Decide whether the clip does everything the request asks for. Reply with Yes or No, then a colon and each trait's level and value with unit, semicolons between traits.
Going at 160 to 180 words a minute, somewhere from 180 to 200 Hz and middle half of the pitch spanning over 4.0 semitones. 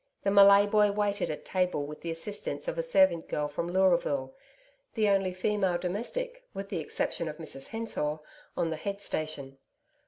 Yes: average, 175 wpm; medium, 185 Hz; average, 4.7 semitones